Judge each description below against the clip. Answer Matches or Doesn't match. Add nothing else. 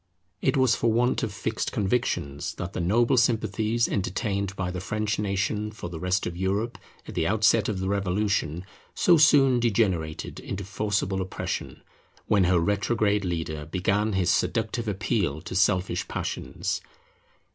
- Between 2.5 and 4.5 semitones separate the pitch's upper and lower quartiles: Matches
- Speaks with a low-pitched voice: Matches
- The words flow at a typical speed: Matches